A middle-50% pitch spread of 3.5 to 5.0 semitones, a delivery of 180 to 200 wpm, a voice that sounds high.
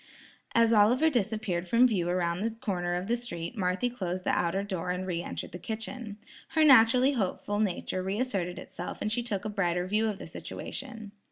Yes: average, 4.3 semitones; average, 195 wpm; high, 205 Hz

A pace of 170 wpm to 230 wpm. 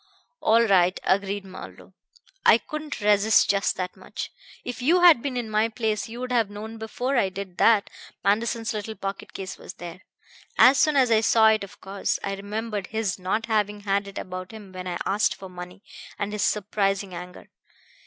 Yes: average, 190 wpm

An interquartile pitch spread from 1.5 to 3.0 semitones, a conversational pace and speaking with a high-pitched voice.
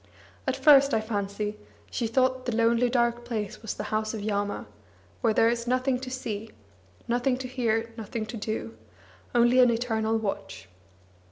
Yes: narrow, 2.4 semitones; average, 165 wpm; high, 230 Hz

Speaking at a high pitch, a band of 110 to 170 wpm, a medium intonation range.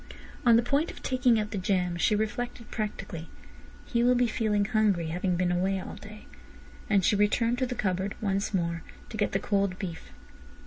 No: high, 205 Hz; average, 190 wpm; average, 3.8 semitones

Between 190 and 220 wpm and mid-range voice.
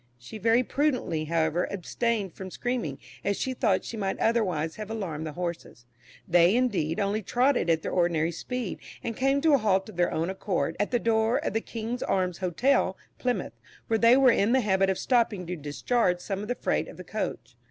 No: fast, 205 wpm; high, 200 Hz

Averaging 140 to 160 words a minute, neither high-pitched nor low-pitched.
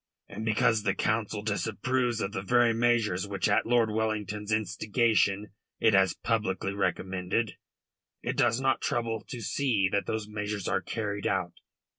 No: average, 150 wpm; low, 105 Hz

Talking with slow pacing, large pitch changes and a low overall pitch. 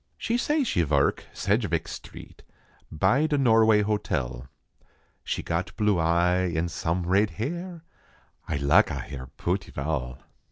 Yes: slow, 130 wpm; wide, 5.9 semitones; very low, 90 Hz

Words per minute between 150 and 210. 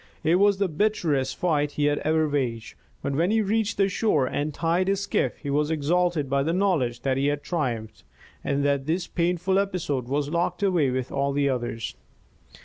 Yes: average, 190 wpm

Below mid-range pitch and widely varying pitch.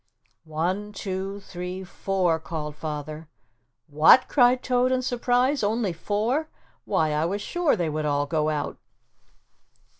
No: medium, 185 Hz; wide, 7.4 semitones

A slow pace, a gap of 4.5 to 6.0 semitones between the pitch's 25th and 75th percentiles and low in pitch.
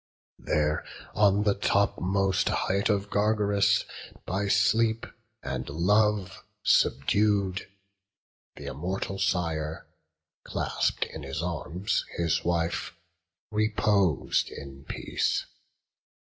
No: slow, 90 wpm; average, 3.7 semitones; very low, 95 Hz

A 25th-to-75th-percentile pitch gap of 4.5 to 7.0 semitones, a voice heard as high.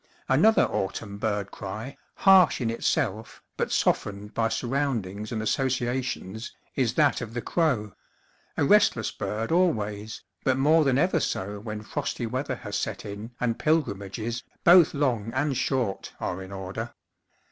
No: average, 5.0 semitones; low, 115 Hz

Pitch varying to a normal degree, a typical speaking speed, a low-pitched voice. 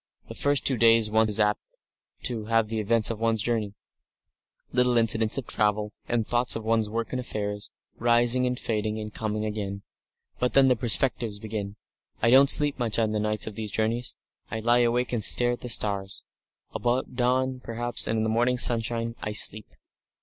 No: narrow, 2.1 semitones; average, 185 wpm; low, 115 Hz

